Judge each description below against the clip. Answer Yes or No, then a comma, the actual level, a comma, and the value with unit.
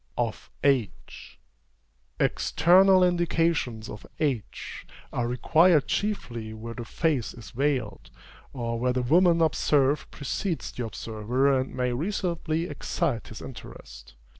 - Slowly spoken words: Yes, slow, 115 wpm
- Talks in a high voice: No, low, 135 Hz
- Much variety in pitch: Yes, wide, 6.1 semitones